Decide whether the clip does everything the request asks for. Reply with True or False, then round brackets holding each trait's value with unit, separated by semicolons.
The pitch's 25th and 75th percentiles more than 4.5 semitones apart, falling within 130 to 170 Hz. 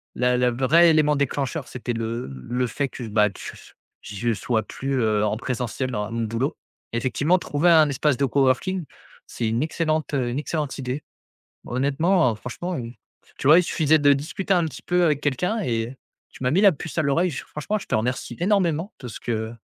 True (4.9 semitones; 135 Hz)